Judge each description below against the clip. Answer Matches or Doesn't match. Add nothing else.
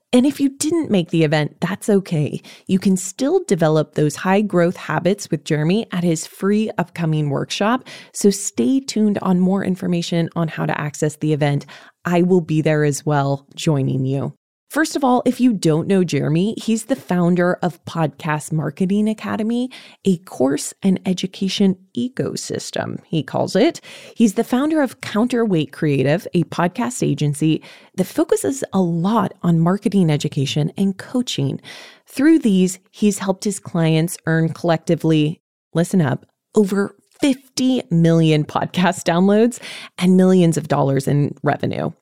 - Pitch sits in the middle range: Matches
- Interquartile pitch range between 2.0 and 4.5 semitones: Doesn't match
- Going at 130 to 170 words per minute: Matches